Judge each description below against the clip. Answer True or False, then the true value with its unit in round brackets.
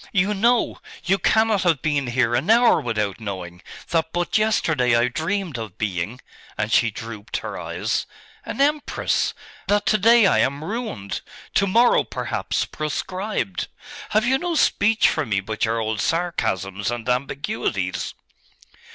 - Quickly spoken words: False (150 wpm)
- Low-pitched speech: False (145 Hz)